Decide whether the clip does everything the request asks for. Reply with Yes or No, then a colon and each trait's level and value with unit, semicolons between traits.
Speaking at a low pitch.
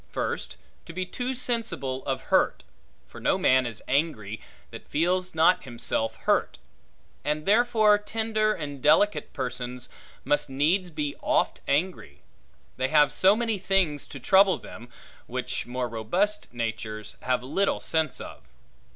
No: medium, 150 Hz